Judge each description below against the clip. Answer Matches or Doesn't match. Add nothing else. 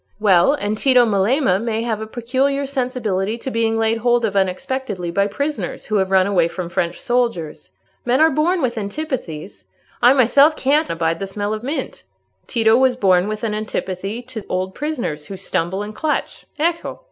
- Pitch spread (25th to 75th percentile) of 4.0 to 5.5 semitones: Matches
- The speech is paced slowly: Doesn't match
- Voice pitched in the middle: Doesn't match